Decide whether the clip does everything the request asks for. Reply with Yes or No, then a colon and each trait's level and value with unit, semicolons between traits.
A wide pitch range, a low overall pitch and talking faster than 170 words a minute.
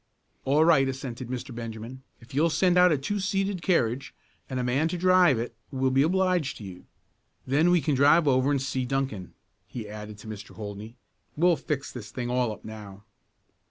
Yes: wide, 5.7 semitones; low, 130 Hz; average, 195 wpm